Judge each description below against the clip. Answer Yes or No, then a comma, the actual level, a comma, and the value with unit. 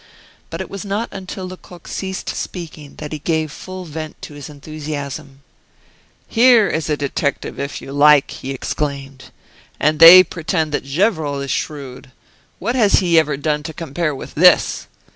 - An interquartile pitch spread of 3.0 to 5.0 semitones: Yes, average, 4.1 semitones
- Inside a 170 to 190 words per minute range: No, average, 160 wpm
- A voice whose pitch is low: No, medium, 155 Hz